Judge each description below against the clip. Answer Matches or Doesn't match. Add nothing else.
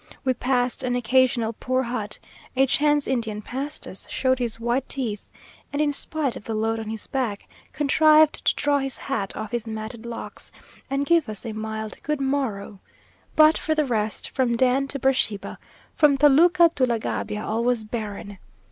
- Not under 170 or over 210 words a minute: Matches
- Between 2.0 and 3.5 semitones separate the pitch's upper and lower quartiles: Doesn't match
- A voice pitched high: Matches